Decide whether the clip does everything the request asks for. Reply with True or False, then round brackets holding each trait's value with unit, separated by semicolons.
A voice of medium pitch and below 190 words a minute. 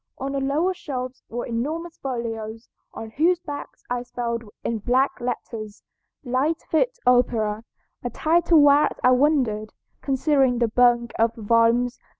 False (250 Hz; 140 wpm)